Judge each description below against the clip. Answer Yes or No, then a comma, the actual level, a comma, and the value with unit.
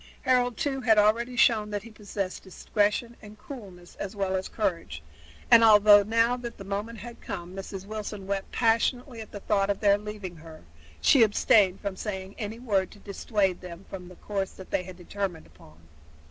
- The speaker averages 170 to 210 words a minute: Yes, average, 185 wpm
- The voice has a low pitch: No, high, 205 Hz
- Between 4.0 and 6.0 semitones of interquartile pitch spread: No, average, 2.9 semitones